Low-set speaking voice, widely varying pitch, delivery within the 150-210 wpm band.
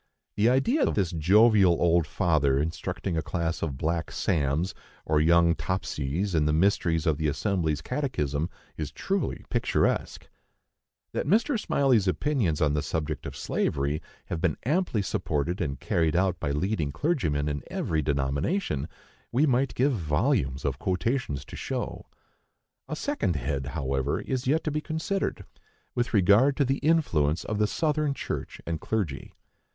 Yes: very low, 85 Hz; wide, 8.4 semitones; average, 155 wpm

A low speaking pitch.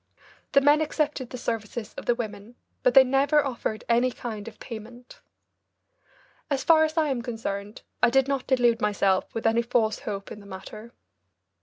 No: high, 235 Hz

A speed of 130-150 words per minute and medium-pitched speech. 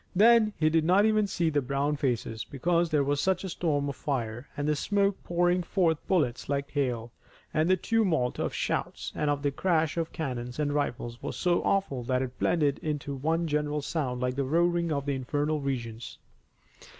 No: average, 190 wpm; medium, 150 Hz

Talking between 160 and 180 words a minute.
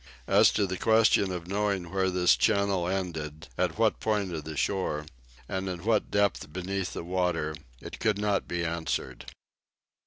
Yes: average, 165 wpm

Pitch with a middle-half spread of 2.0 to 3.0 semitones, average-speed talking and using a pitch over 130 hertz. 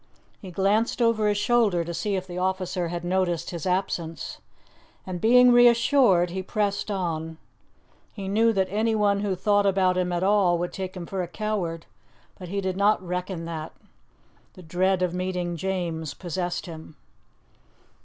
Yes: average, 2.7 semitones; average, 165 wpm; medium, 185 Hz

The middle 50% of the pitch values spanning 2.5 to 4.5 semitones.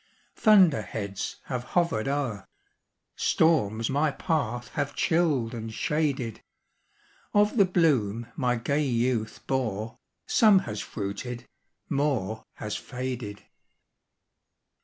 No: wide, 5.5 semitones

